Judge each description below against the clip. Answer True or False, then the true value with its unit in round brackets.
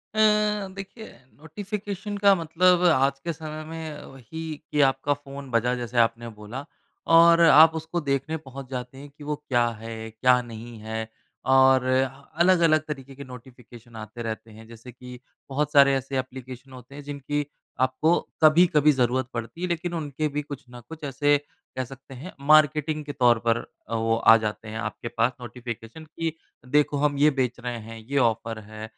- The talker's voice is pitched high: False (135 Hz)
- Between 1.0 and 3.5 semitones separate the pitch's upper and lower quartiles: False (4.2 semitones)